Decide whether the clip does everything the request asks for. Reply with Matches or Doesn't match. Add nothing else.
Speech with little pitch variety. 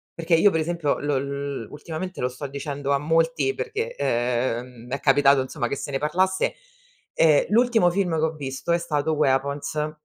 Doesn't match